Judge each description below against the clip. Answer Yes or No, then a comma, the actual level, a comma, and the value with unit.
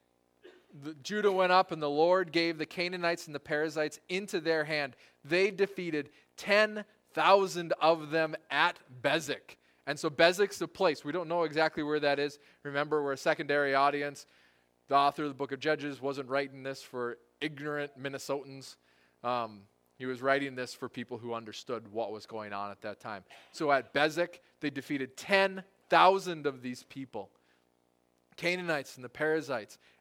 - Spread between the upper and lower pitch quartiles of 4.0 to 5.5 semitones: Yes, average, 4.6 semitones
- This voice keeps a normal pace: Yes, average, 165 wpm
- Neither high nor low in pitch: Yes, medium, 145 Hz